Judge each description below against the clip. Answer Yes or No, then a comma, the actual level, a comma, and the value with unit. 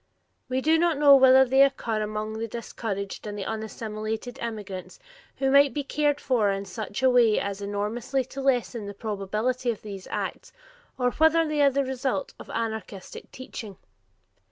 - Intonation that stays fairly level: No, average, 4.1 semitones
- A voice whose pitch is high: Yes, high, 235 Hz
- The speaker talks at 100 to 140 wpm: No, average, 165 wpm